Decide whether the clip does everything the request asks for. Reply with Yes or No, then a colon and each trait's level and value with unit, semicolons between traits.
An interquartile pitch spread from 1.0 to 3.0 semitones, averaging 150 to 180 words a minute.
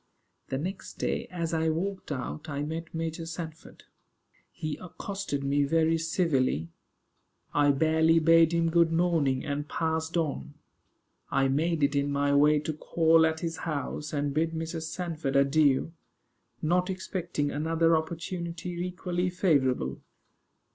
No: narrow, 2.6 semitones; slow, 135 wpm